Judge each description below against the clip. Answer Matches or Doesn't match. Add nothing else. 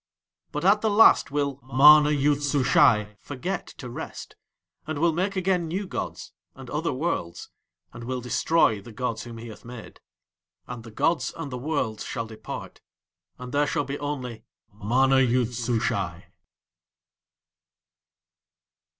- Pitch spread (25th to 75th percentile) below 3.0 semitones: Doesn't match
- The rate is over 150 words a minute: Doesn't match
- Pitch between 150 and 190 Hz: Doesn't match